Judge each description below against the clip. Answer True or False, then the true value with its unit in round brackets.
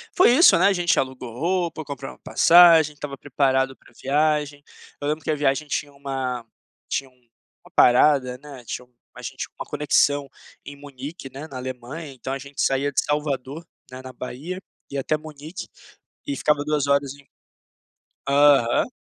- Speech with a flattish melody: True (2.3 semitones)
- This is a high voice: False (140 Hz)